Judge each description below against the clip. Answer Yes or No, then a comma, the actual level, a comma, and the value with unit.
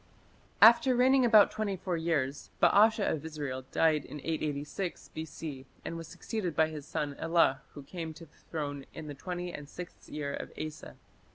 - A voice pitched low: No, medium, 160 Hz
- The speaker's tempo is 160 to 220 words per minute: Yes, average, 175 wpm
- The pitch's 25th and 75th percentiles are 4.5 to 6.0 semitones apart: No, average, 3.6 semitones